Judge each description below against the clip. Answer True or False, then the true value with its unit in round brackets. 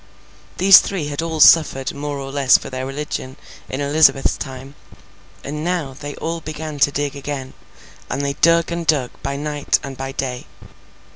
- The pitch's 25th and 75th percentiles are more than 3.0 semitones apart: False (2.5 semitones)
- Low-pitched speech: False (145 Hz)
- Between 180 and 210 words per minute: False (170 wpm)